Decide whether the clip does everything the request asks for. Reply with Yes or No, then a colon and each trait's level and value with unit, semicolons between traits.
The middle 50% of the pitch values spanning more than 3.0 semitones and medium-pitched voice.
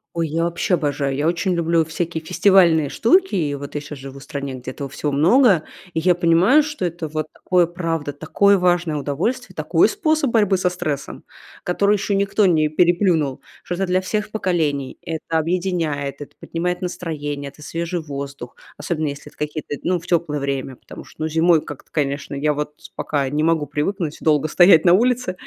Yes: average, 3.6 semitones; medium, 165 Hz